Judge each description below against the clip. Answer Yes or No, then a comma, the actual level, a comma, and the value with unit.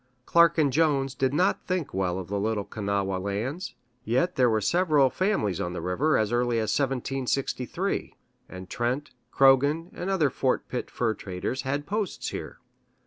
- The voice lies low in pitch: Yes, low, 130 Hz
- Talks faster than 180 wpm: No, average, 160 wpm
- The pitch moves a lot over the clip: Yes, wide, 6.1 semitones